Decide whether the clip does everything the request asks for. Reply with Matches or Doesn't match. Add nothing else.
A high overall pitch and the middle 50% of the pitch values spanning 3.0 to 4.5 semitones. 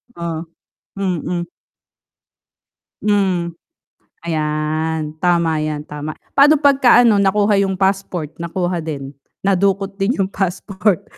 Doesn't match